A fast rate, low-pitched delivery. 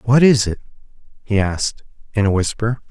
No: average, 165 wpm; low, 110 Hz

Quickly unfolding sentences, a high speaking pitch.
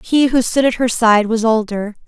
Yes: fast, 230 wpm; high, 230 Hz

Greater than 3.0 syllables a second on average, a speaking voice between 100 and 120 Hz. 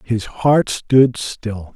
No: 2.4 syllables/s; low, 115 Hz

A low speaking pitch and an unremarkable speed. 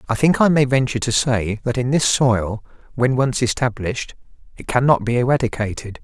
Yes: low, 120 Hz; average, 180 wpm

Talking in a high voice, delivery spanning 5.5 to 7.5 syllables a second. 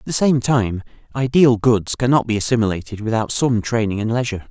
No: low, 115 Hz; 5.8 syllables/s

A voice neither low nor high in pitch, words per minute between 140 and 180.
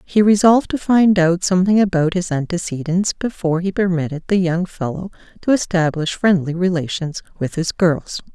Yes: medium, 180 Hz; average, 160 wpm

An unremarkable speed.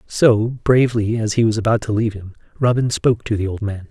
No: fast, 230 wpm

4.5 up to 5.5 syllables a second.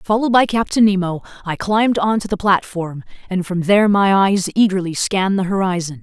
No: 5.7 syllables/s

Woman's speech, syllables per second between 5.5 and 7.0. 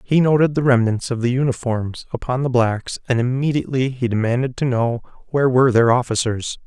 No: male; 5.7 syllables/s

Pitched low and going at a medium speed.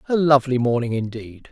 Yes: low, 125 Hz; average, 160 wpm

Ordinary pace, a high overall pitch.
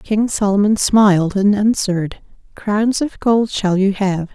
Yes: average, 150 wpm; high, 205 Hz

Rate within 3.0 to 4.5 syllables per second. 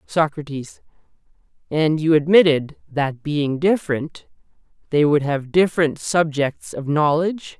Yes: 4.3 syllables/s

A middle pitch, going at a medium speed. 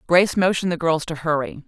No: medium, 165 Hz; fast, 215 wpm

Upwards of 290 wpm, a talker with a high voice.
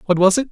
Yes: fast, 345 wpm; high, 200 Hz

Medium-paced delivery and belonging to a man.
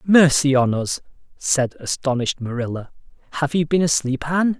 Yes: average, 145 wpm; male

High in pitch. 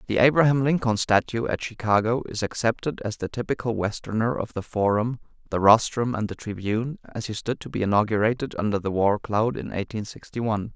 No: low, 110 Hz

